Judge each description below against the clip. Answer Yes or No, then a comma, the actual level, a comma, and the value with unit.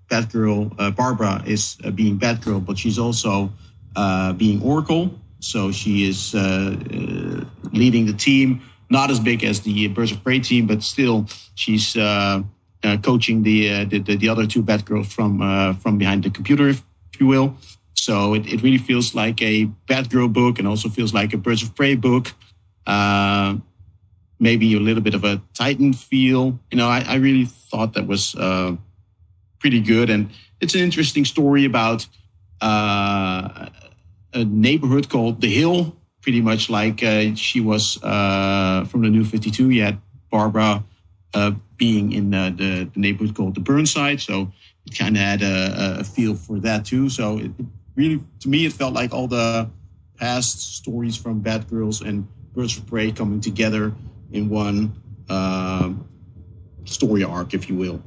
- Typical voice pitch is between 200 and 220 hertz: No, low, 110 Hz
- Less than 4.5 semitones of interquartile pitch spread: Yes, average, 3.1 semitones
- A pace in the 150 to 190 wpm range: Yes, average, 175 wpm